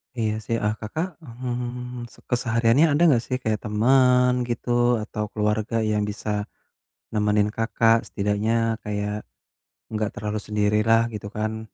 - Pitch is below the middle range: Yes, low, 110 Hz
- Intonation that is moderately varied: No, narrow, 2.3 semitones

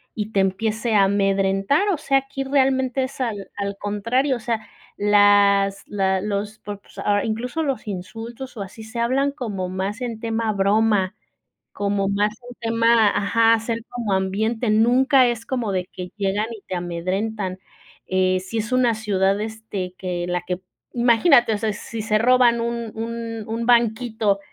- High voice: Yes, high, 220 Hz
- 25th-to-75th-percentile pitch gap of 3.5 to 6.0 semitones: No, average, 3.0 semitones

